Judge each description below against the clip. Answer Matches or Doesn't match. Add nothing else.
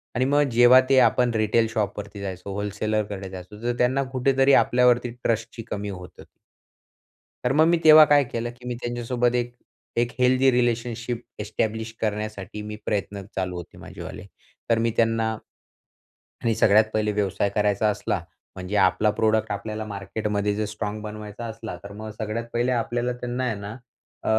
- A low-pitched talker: Matches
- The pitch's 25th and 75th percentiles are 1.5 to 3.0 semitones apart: Matches